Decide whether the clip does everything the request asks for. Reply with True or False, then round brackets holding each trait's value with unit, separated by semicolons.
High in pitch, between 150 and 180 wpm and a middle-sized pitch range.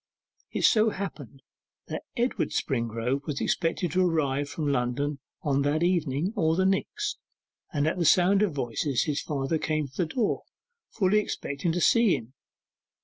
False (155 Hz; 165 wpm; 5.0 semitones)